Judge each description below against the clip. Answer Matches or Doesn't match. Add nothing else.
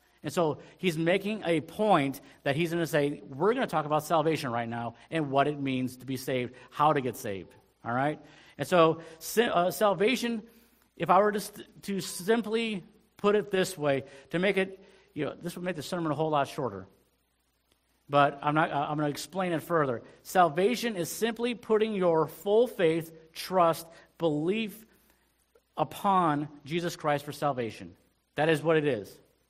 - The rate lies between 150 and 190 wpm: Matches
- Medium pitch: Matches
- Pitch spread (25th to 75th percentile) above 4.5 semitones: Matches